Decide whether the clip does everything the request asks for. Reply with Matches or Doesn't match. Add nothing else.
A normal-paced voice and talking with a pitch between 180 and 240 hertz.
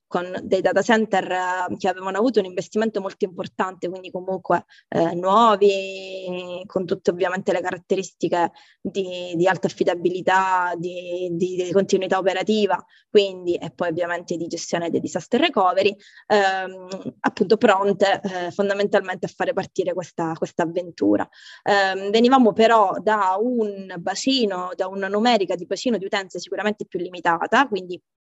Matches